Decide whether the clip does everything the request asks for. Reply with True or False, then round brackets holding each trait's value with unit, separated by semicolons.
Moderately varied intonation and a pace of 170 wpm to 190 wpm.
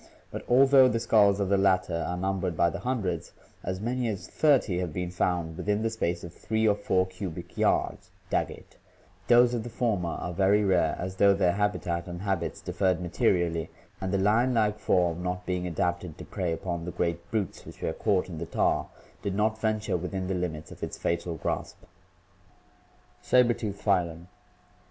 True (3.3 semitones; 185 wpm)